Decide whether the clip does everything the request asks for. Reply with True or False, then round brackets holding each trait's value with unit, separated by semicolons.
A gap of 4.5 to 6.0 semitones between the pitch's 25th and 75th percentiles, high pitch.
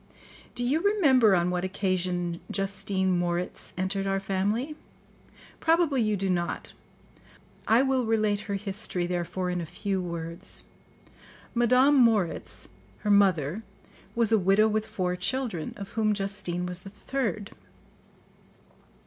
False (3.7 semitones; 195 Hz)